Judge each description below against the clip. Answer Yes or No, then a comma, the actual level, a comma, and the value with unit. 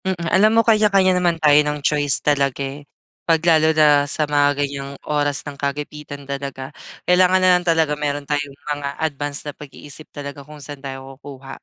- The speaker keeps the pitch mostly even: Yes, narrow, 2.0 semitones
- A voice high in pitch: No, medium, 145 Hz